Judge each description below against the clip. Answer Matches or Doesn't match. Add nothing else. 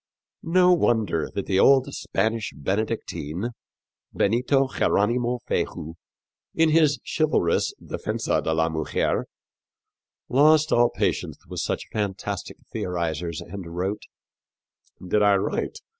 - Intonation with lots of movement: Matches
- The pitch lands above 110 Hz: Doesn't match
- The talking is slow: Matches